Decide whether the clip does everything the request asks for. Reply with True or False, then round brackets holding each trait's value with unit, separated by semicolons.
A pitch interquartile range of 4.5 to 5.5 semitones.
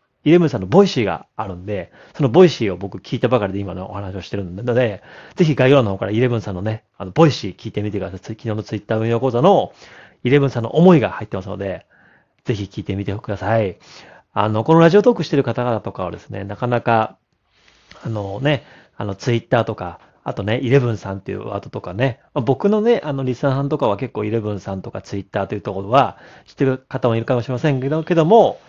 True (5.2 semitones)